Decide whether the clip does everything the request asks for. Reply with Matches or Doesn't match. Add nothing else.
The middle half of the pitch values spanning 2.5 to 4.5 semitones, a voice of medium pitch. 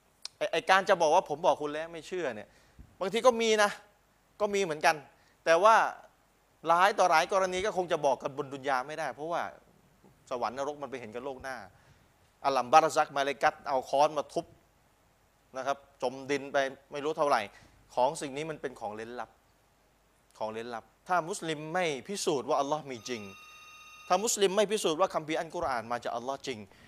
Doesn't match